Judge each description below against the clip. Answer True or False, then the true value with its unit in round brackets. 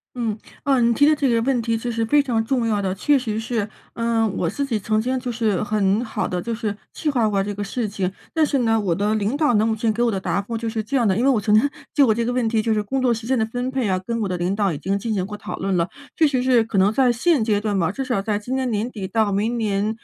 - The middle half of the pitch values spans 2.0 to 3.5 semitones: True (3.1 semitones)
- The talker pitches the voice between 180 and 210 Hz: False (225 Hz)